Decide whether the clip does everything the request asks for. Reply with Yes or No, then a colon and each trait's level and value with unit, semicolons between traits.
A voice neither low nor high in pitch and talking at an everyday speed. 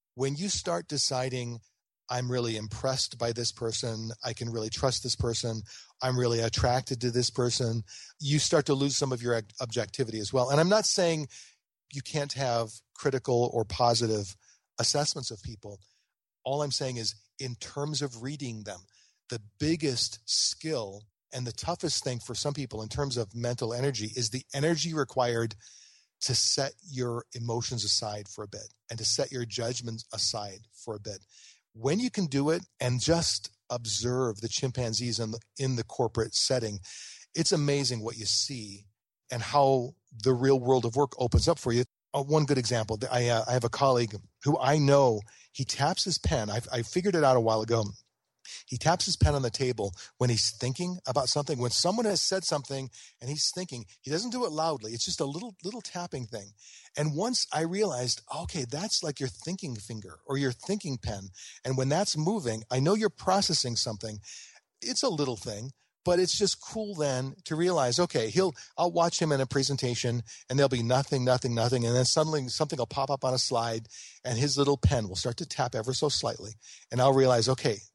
No: low, 125 Hz; average, 195 wpm